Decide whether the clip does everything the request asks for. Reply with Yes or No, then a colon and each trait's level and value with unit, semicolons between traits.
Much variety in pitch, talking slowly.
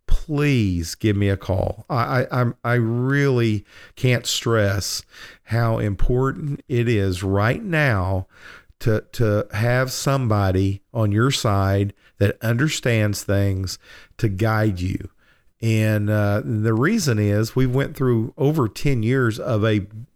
No: average, 3.9 semitones; slow, 130 wpm